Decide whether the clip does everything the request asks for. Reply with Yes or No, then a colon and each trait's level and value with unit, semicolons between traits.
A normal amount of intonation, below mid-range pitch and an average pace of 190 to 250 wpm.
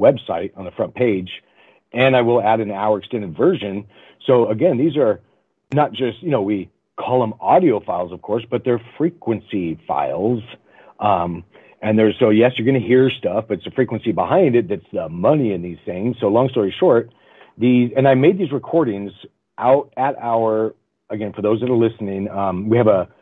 Yes: average, 3.5 semitones; low, 115 Hz; average, 200 wpm